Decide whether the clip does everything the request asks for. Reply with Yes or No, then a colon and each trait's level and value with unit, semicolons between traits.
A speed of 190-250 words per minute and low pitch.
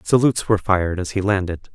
Yes: fast, 205 wpm; low, 100 Hz